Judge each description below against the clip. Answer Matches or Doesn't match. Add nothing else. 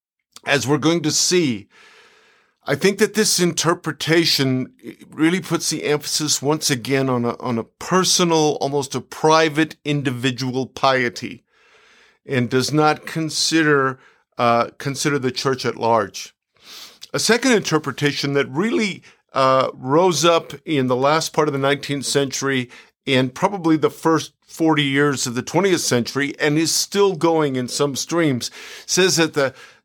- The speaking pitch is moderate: Matches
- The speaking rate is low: Doesn't match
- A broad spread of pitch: Doesn't match